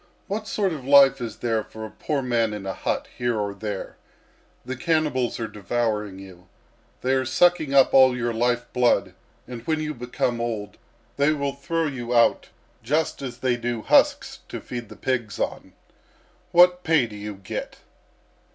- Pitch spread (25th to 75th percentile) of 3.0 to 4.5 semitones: Yes, average, 4.0 semitones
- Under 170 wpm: No, average, 175 wpm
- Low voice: Yes, low, 125 Hz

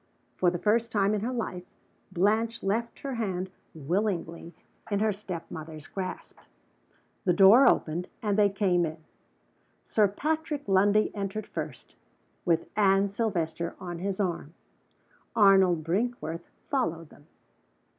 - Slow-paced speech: Yes, slow, 130 wpm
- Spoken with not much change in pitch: No, average, 3.6 semitones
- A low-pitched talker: No, high, 195 Hz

